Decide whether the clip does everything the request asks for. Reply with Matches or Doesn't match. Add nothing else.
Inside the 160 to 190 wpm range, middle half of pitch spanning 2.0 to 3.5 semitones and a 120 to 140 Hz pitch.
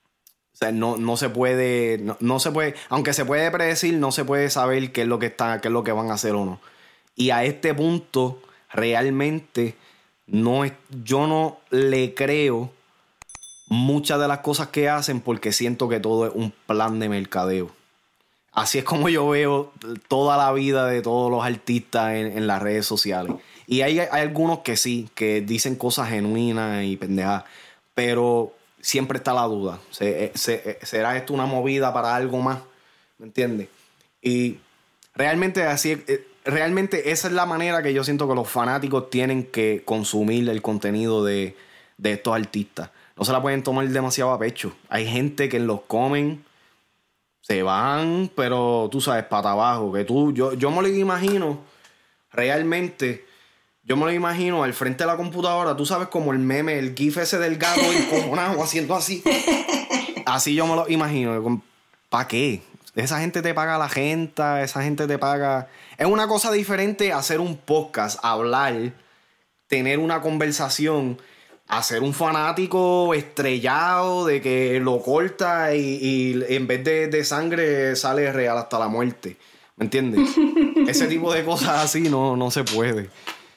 Doesn't match